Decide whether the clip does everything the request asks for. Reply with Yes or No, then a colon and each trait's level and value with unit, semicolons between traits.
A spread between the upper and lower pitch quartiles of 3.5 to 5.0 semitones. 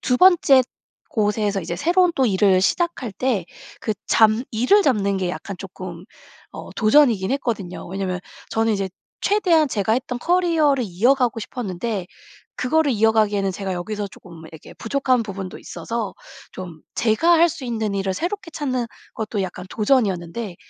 No: wide, 5.5 semitones